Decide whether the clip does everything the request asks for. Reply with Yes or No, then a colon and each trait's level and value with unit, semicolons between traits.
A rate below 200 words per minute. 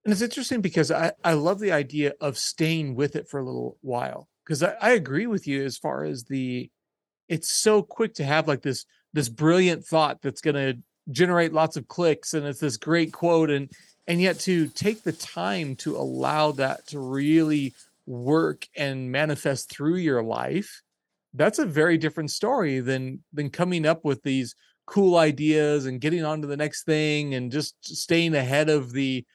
Yes: average, 190 wpm